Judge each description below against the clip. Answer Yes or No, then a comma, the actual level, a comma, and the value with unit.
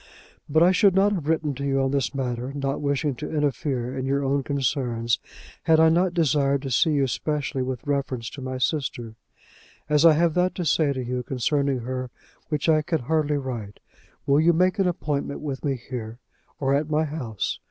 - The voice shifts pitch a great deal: No, average, 3.2 semitones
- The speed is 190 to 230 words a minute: Yes, average, 200 wpm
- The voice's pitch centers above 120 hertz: Yes, medium, 140 Hz